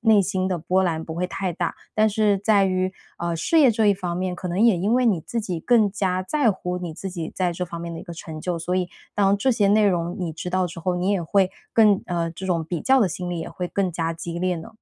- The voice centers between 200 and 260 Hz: No, medium, 185 Hz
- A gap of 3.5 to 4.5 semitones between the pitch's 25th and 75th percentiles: No, average, 2.8 semitones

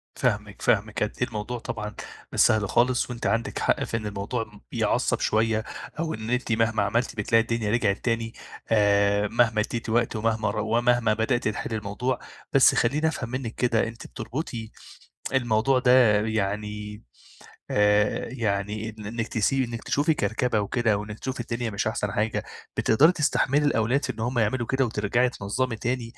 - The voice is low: Yes, low, 115 Hz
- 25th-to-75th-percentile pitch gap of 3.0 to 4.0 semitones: No, narrow, 2.6 semitones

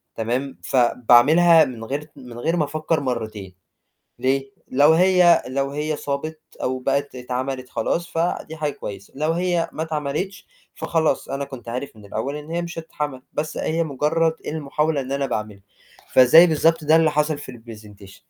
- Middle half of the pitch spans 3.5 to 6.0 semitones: Yes, average, 4.1 semitones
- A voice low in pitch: No, medium, 145 Hz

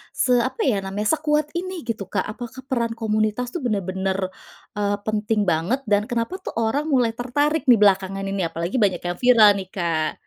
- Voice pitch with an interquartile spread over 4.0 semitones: Yes, average, 4.5 semitones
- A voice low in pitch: No, high, 215 Hz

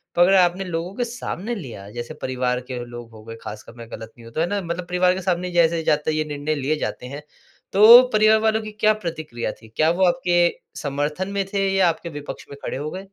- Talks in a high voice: No, medium, 165 Hz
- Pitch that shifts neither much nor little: No, wide, 6.0 semitones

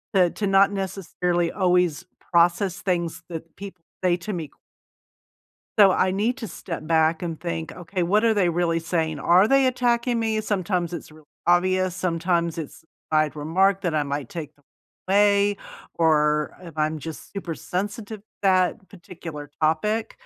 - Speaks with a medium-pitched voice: Yes, medium, 180 Hz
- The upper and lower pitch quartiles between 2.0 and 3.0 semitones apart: No, average, 3.4 semitones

